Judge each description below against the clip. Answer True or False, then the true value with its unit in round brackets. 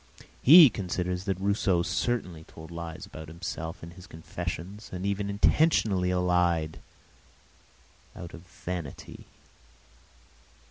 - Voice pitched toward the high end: False (90 Hz)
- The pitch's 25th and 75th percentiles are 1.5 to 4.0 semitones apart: True (2.9 semitones)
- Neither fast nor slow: False (105 wpm)